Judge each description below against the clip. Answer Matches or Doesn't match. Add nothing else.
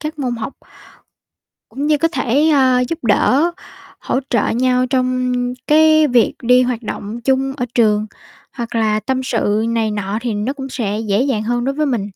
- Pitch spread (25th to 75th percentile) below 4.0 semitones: Matches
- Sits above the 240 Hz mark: Matches